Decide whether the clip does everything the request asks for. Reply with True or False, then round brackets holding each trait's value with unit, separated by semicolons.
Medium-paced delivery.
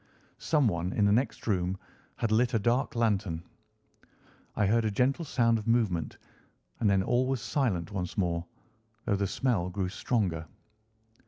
True (155 wpm)